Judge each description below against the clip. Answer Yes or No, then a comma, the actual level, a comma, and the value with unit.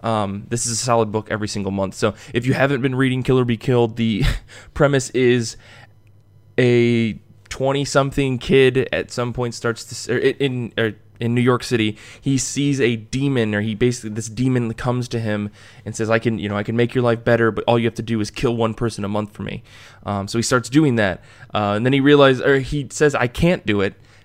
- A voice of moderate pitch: No, low, 115 Hz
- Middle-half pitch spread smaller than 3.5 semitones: Yes, average, 2.7 semitones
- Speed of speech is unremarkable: No, fast, 230 wpm